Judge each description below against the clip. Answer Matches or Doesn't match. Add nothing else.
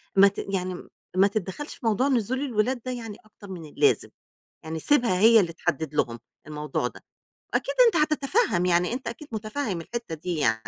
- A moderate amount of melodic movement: Doesn't match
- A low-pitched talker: Doesn't match